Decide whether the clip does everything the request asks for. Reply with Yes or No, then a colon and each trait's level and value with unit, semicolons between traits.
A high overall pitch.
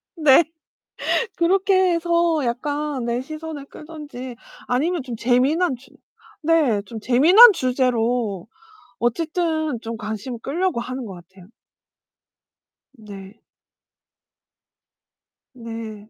Yes: very high, 260 Hz